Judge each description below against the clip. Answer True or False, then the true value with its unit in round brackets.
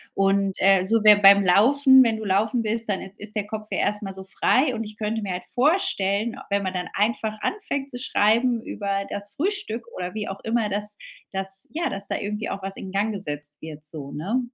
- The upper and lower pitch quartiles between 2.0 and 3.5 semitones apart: True (2.8 semitones)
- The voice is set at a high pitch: True (210 Hz)